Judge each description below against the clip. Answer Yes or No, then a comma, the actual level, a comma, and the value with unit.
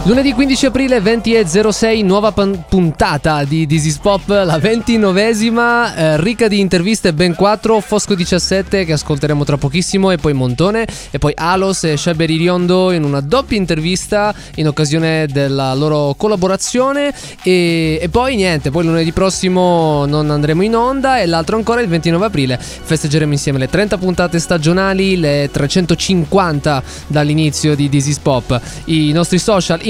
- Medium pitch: Yes, medium, 180 Hz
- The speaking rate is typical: Yes, average, 145 wpm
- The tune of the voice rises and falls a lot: No, average, 5.0 semitones